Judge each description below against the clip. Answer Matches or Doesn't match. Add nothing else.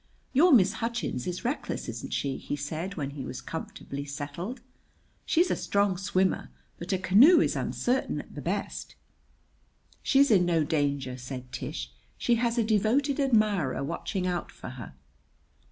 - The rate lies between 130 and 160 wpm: Matches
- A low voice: Doesn't match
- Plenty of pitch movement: Matches